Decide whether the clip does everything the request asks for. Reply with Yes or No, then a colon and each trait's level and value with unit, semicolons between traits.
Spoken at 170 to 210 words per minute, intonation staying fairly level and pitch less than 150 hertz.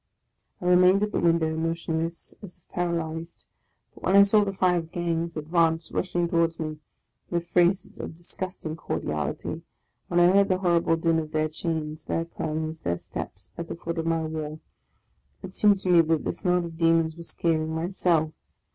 No: average, 190 wpm; narrow, 1.7 semitones; medium, 165 Hz